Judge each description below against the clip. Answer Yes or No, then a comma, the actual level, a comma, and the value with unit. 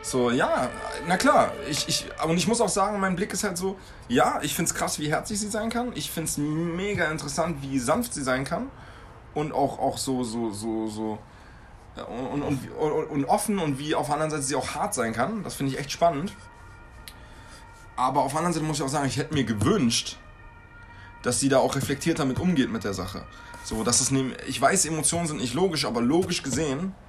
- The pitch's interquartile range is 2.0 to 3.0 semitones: No, wide, 5.6 semitones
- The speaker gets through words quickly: Yes, fast, 215 wpm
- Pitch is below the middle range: No, medium, 145 Hz